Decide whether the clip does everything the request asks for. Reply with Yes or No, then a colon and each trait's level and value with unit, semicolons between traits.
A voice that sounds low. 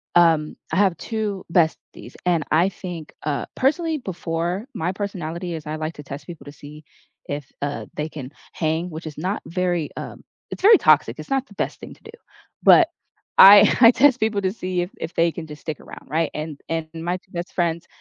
No: medium, 170 Hz